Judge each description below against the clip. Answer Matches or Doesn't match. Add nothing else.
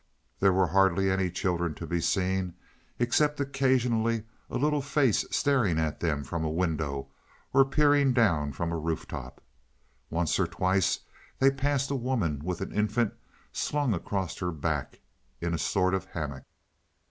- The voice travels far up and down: Matches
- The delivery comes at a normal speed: Matches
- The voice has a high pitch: Doesn't match